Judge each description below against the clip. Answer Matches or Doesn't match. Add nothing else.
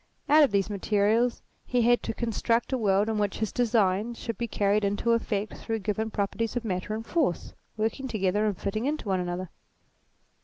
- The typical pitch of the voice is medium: Doesn't match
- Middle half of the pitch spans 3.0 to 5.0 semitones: Doesn't match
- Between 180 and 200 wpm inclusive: Matches